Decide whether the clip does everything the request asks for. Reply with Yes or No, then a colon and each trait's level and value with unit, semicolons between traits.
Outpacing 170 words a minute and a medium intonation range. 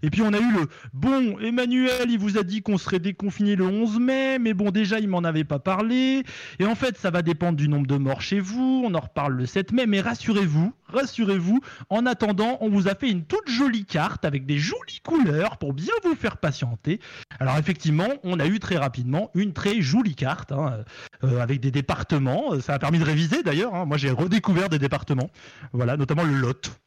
No: fast, 220 wpm; wide, 7.0 semitones